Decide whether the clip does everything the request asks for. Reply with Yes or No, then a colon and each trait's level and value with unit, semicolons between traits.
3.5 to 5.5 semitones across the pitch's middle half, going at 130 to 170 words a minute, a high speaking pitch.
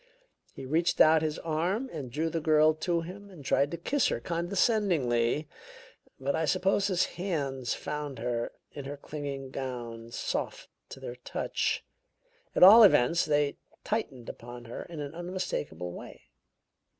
No: average, 4.9 semitones; average, 150 wpm; medium, 150 Hz